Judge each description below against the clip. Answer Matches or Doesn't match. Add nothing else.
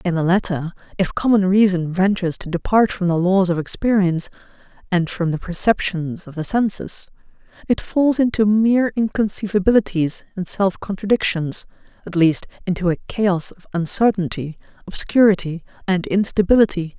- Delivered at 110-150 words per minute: Matches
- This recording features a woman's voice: Matches